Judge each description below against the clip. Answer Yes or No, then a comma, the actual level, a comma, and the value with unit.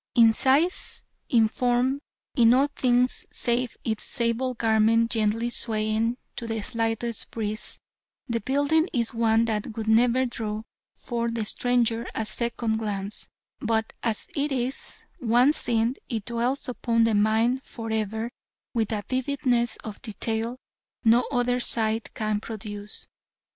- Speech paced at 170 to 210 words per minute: No, average, 140 wpm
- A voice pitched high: Yes, high, 230 Hz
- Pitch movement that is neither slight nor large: No, narrow, 1.9 semitones